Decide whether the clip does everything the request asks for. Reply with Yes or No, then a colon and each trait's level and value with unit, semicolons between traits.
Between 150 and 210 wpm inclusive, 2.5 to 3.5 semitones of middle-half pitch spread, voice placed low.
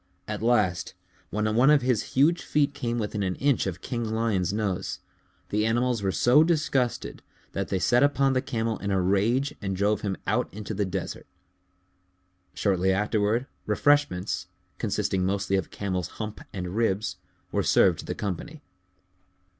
No: average, 160 wpm; average, 4.2 semitones; low, 105 Hz